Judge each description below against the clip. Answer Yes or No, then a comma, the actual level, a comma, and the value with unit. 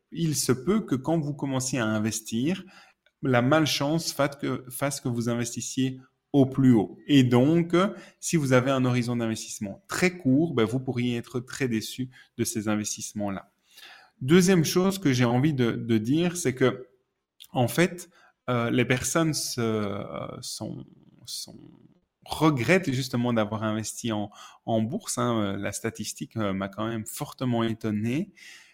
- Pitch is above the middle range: No, low, 125 Hz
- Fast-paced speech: No, average, 150 wpm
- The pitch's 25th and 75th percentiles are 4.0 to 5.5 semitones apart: Yes, average, 4.5 semitones